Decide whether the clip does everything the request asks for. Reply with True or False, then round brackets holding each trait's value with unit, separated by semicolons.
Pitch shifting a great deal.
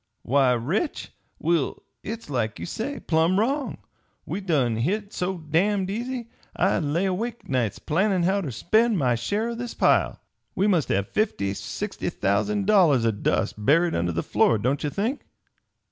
True (8.7 semitones)